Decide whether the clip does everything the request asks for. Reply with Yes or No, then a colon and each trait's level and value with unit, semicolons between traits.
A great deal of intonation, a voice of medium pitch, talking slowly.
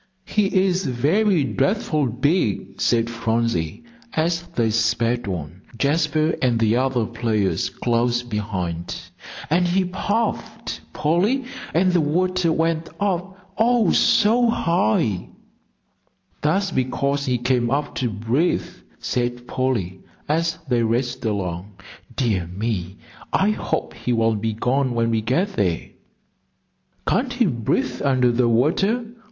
No: wide, 7.2 semitones; low, 125 Hz; slow, 125 wpm